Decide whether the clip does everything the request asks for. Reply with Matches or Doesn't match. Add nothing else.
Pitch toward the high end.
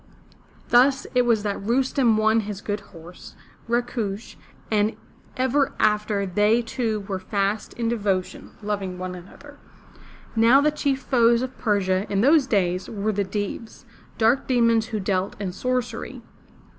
Matches